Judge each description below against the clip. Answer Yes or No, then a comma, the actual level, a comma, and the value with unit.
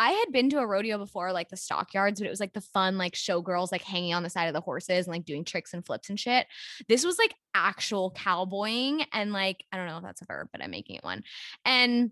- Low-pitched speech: No, high, 195 Hz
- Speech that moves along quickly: Yes, fast, 265 wpm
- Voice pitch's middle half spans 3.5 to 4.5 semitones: Yes, average, 4.1 semitones